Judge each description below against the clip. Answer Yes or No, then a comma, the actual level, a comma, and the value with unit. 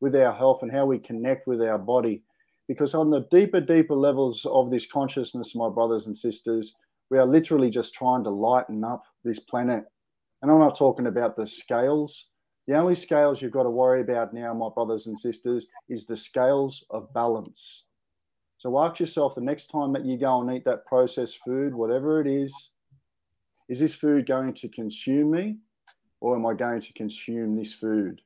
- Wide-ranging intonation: No, average, 3.6 semitones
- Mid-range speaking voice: No, low, 125 Hz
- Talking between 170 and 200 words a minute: Yes, average, 190 wpm